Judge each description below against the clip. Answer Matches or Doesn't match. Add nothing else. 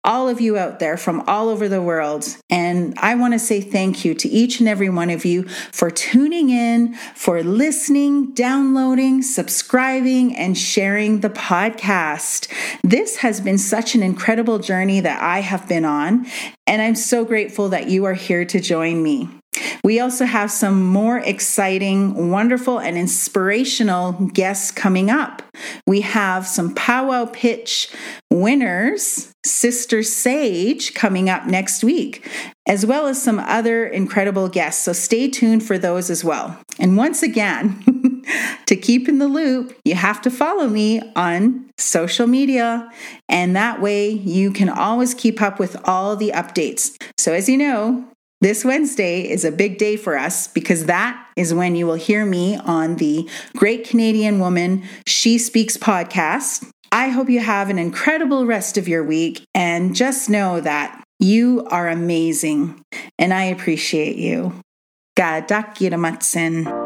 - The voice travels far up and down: Doesn't match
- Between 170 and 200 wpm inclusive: Doesn't match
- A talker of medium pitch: Doesn't match